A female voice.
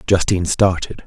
No: male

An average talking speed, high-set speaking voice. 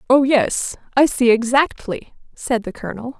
Yes: average, 150 wpm; high, 245 Hz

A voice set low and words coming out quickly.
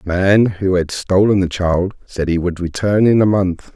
Yes: very low, 95 Hz; fast, 225 wpm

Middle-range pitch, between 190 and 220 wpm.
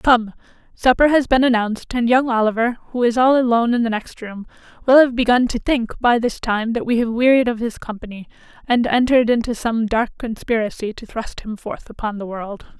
No: high, 235 Hz; fast, 205 wpm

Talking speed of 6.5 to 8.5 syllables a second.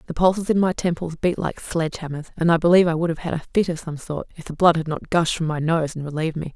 Yes: 6.8 syllables/s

